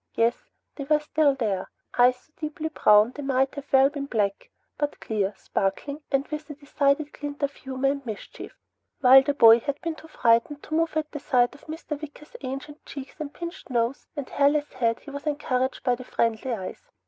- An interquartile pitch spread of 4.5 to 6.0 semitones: No, average, 3.3 semitones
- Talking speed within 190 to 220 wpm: Yes, average, 195 wpm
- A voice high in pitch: Yes, very high, 275 Hz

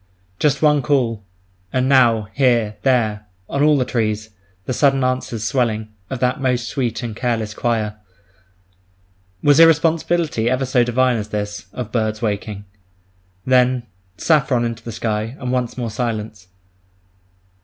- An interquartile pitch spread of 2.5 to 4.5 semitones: Yes, average, 3.3 semitones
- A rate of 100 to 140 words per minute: Yes, slow, 135 wpm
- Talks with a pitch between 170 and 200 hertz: No, low, 120 Hz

